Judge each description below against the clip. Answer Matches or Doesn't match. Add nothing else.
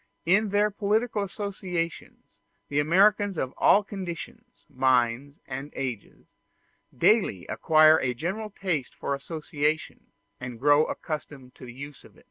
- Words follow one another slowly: Matches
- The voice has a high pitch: Doesn't match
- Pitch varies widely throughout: Matches